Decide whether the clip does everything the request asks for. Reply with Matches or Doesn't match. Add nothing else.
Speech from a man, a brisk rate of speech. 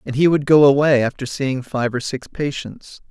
Matches